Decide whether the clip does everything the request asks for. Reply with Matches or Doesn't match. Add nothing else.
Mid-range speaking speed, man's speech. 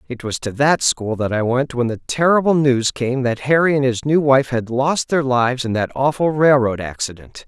Doesn't match